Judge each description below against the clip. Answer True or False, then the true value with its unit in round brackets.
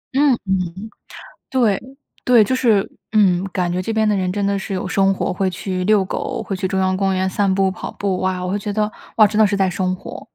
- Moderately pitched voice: False (195 Hz)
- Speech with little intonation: True (2.1 semitones)